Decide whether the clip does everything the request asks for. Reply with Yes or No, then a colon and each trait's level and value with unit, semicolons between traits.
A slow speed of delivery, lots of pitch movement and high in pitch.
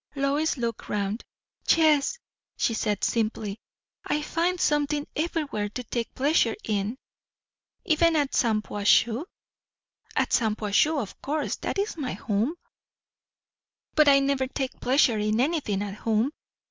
Yes: slow, 125 wpm; wide, 5.8 semitones; very high, 260 Hz